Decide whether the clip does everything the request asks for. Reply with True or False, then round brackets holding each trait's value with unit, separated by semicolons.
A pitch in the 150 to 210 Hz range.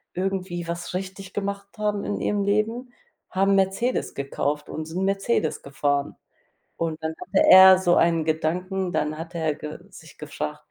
True (185 Hz)